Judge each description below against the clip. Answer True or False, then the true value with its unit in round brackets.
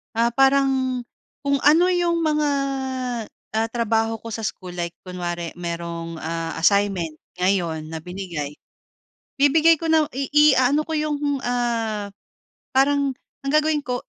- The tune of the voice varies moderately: False (8.2 semitones)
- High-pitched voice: True (230 Hz)